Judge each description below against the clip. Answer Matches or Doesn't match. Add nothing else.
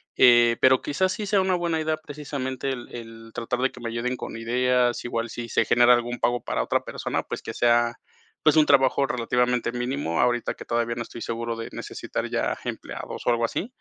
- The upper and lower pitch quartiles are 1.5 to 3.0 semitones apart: Matches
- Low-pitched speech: Matches